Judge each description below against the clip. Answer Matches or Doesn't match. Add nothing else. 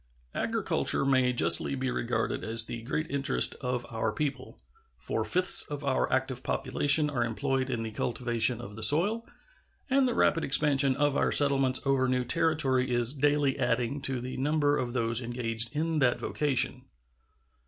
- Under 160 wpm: Doesn't match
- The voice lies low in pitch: Matches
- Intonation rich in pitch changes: Doesn't match